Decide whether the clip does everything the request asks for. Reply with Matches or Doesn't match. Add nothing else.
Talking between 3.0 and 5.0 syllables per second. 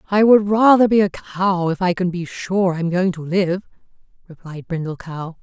Matches